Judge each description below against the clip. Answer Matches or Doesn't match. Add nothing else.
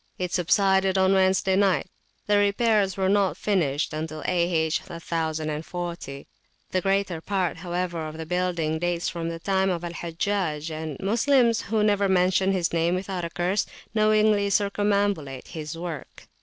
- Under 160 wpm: Matches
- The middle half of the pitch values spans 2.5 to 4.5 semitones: Matches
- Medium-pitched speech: Matches